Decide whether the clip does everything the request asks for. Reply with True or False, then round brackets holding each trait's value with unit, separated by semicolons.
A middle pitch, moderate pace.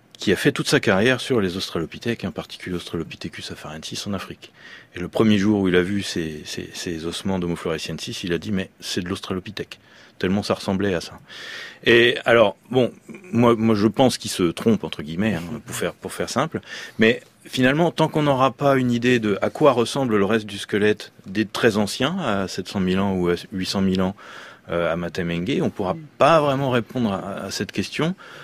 False (105 Hz; 205 wpm)